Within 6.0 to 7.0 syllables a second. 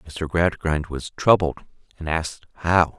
No: 4.3 syllables/s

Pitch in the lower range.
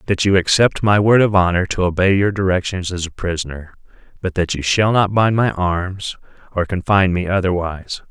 Yes: very low, 95 Hz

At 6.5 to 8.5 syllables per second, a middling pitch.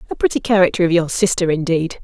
Yes: 6.7 syllables/s; medium, 170 Hz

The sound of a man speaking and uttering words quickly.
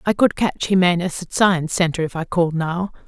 No: female; fast, 215 wpm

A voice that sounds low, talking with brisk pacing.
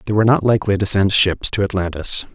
Yes: low, 100 Hz; fast, 230 wpm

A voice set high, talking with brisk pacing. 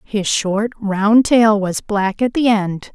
No: high, 210 Hz; average, 185 wpm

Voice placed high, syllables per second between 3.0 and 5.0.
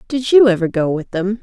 No: high, 205 Hz; 5.5 syllables/s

